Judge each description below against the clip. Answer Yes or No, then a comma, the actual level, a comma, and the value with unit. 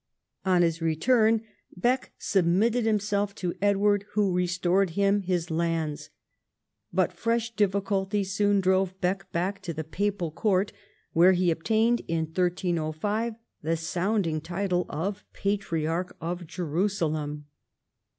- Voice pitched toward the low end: No, medium, 185 Hz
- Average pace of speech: No, slow, 120 wpm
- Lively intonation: No, average, 3.3 semitones